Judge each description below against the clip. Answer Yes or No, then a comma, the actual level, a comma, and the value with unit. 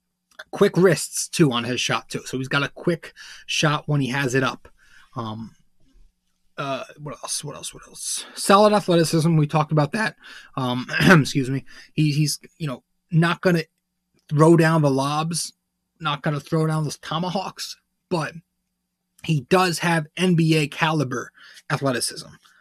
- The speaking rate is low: No, average, 155 wpm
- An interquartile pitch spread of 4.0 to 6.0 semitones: Yes, average, 4.3 semitones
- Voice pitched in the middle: Yes, medium, 160 Hz